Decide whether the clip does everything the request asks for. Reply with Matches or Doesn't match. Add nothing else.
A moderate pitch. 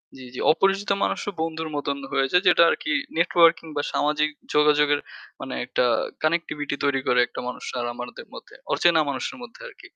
Matches